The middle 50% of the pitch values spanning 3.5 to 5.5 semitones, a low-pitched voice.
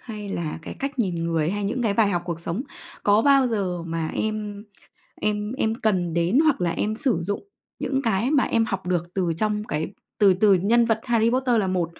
No: average, 4.3 semitones; high, 205 Hz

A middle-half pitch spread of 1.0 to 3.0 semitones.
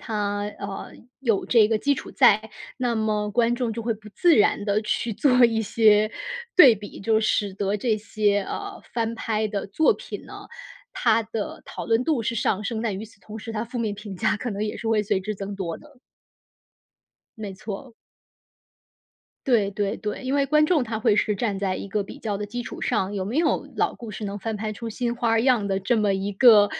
Yes: narrow, 2.4 semitones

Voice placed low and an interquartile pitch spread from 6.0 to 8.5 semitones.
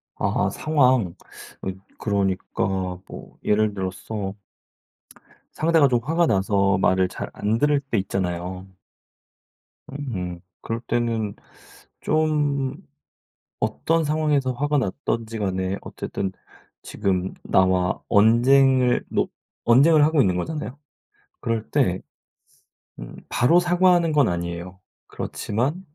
Yes: low, 115 Hz; wide, 7.3 semitones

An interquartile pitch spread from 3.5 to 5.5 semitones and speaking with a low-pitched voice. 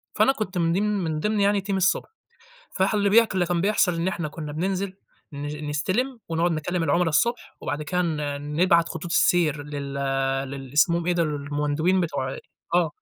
No: average, 3.9 semitones; medium, 170 Hz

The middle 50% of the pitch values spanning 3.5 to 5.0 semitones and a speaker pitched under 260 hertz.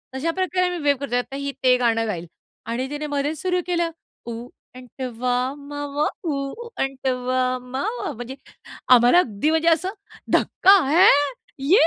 No: average, 4.3 semitones; very high, 275 Hz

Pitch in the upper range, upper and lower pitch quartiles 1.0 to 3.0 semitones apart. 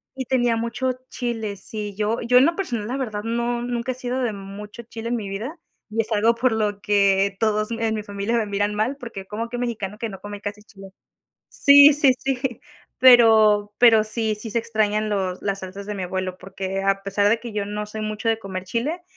Yes: high, 215 Hz; average, 2.7 semitones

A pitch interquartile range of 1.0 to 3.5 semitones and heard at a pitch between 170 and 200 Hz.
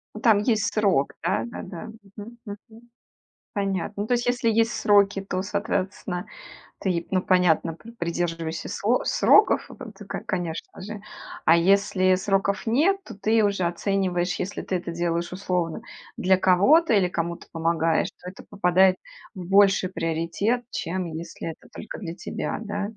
Yes: average, 3.2 semitones; high, 190 Hz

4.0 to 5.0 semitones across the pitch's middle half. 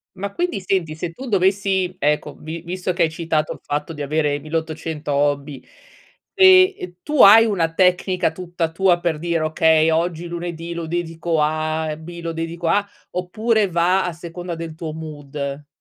No: narrow, 2.5 semitones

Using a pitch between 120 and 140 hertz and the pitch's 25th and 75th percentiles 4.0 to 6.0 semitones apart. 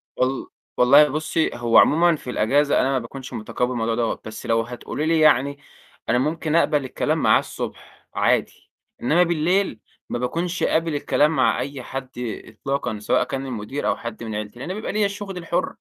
Yes: low, 135 Hz; average, 4.9 semitones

